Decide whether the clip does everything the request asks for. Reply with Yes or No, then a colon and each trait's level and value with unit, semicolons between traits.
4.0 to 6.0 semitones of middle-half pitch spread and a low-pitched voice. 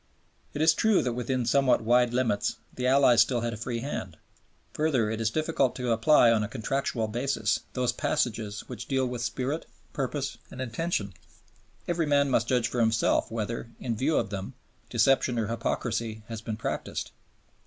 No: average, 3.1 semitones; low, 120 Hz